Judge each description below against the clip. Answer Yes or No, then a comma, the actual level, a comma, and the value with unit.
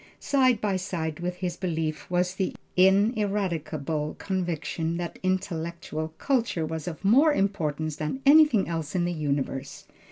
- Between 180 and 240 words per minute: No, slow, 135 wpm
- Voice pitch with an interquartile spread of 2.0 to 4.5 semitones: Yes, average, 3.7 semitones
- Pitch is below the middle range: No, medium, 175 Hz